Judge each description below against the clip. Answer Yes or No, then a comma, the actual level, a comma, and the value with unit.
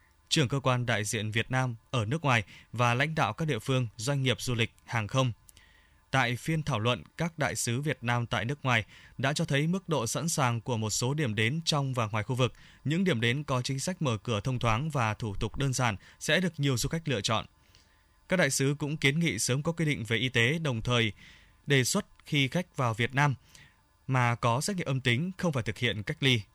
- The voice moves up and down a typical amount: Yes, average, 4.3 semitones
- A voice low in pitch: Yes, low, 125 Hz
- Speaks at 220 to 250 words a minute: Yes, average, 240 wpm